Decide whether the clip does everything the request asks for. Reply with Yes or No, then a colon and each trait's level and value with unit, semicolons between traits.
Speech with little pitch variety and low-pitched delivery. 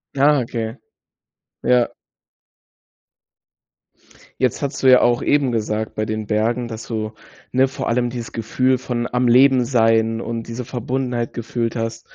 Yes: narrow, 2.0 semitones; low, 120 Hz